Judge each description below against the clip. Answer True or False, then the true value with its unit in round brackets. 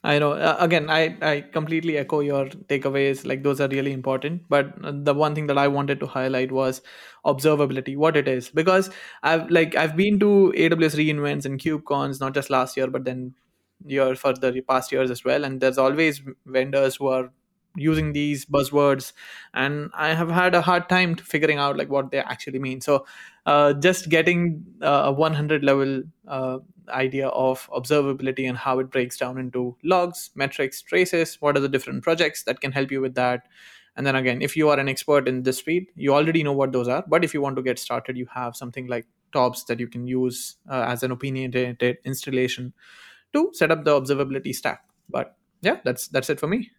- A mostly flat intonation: False (3.2 semitones)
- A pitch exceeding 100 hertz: True (140 Hz)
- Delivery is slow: False (200 wpm)